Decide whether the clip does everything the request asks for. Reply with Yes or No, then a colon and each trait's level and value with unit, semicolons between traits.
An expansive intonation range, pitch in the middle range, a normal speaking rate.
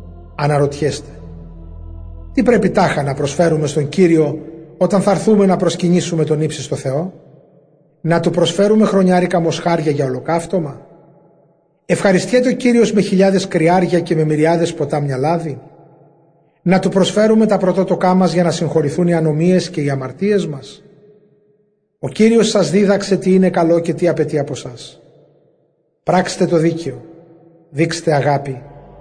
No: average, 3.9 semitones; medium, 170 Hz; average, 135 wpm